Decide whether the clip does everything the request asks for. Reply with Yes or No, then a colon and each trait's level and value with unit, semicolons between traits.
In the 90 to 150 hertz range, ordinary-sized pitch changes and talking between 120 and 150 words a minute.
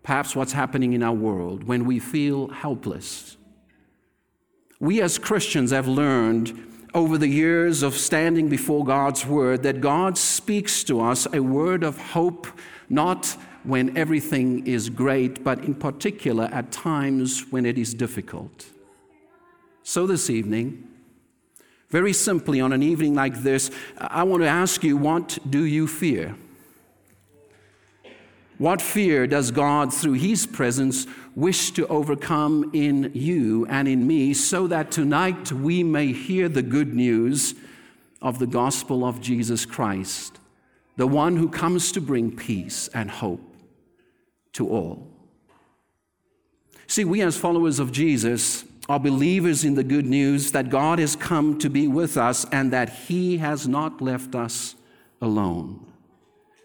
Yes: medium, 140 Hz; average, 4.7 semitones; average, 140 wpm